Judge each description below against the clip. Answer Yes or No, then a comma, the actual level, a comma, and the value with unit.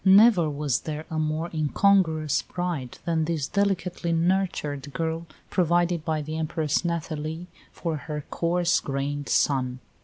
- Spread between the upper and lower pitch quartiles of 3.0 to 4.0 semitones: No, narrow, 2.5 semitones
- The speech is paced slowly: Yes, slow, 130 wpm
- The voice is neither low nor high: Yes, medium, 160 Hz